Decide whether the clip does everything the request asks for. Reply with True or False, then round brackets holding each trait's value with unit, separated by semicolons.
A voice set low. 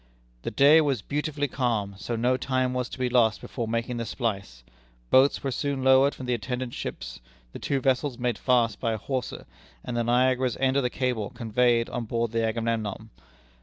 True (125 Hz)